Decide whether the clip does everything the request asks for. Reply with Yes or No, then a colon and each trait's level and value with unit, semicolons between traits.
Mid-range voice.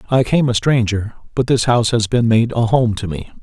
No: low, 115 Hz